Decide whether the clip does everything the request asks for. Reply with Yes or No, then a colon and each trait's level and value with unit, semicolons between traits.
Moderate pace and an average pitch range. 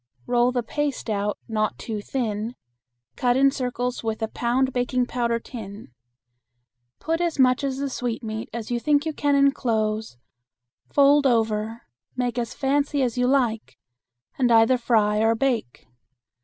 Yes: average, 150 wpm; average, 3.2 semitones